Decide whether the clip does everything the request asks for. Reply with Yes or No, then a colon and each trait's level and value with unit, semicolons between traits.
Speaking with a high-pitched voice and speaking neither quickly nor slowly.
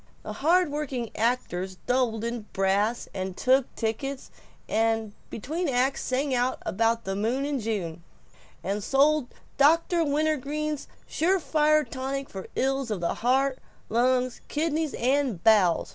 No: very high, 255 Hz; slow, 130 wpm